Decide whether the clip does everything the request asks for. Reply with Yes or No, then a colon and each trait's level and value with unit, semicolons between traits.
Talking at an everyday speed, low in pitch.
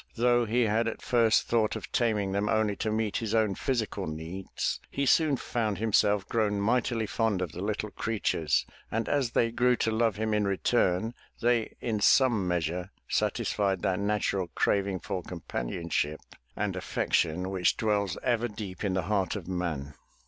Yes: average, 170 wpm; low, 105 Hz